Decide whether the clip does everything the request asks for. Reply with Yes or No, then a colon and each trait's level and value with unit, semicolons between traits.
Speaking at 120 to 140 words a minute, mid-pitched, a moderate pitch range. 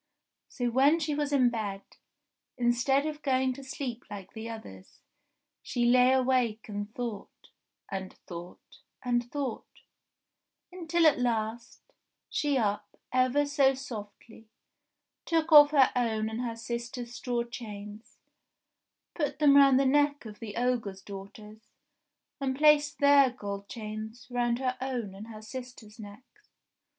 No: slow, 135 wpm; high, 245 Hz; average, 3.9 semitones